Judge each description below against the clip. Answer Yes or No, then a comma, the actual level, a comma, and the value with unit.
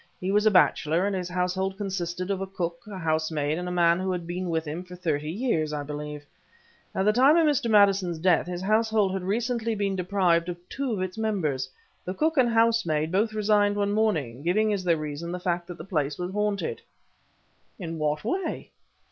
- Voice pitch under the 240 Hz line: Yes, medium, 185 Hz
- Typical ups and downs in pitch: Yes, average, 3.7 semitones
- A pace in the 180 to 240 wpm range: Yes, fast, 205 wpm